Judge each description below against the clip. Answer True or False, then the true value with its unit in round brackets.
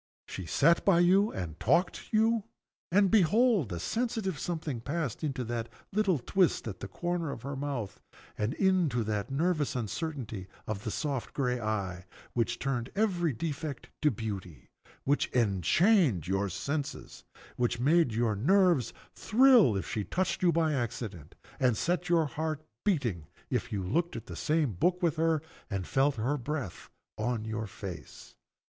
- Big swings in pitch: True (7.9 semitones)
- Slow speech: False (155 wpm)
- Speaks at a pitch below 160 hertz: True (140 Hz)